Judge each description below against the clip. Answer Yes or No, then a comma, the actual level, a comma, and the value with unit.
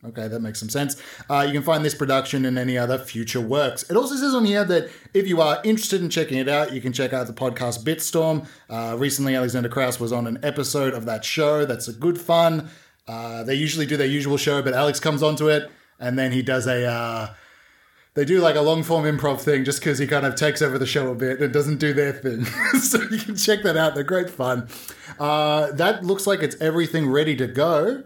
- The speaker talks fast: Yes, fast, 240 wpm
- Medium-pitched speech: Yes, medium, 145 Hz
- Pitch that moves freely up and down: No, average, 3.7 semitones